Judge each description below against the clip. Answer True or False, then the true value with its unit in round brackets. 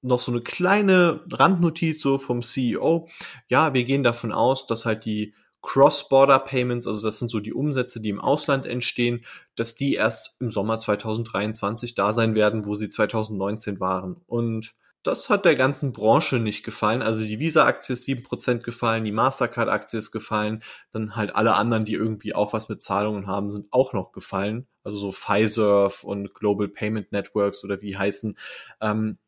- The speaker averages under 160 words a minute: False (170 wpm)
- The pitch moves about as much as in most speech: True (3.3 semitones)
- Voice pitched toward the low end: True (110 Hz)